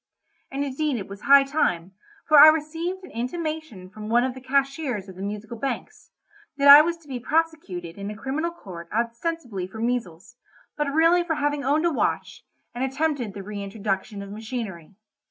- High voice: Yes, very high, 255 Hz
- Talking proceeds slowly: No, average, 180 wpm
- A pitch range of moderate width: No, wide, 6.9 semitones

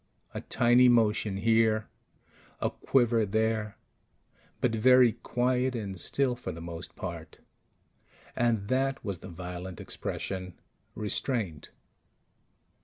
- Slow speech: Yes, slow, 105 wpm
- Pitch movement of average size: Yes, average, 4.1 semitones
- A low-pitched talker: Yes, low, 110 Hz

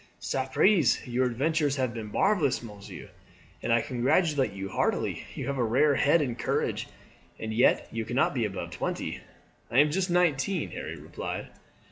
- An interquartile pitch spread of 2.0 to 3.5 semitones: No, average, 4.4 semitones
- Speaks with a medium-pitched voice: No, low, 130 Hz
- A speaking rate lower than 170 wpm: Yes, average, 160 wpm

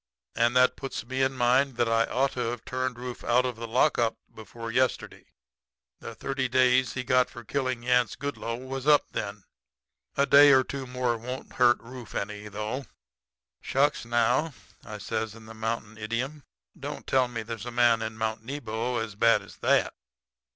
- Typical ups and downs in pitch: No, narrow, 2.3 semitones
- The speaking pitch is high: No, low, 120 Hz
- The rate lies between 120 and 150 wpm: No, average, 180 wpm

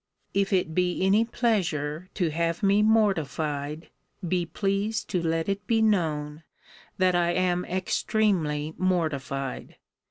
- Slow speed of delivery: Yes, slow, 125 wpm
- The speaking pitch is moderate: Yes, medium, 180 Hz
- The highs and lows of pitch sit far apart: No, average, 4.0 semitones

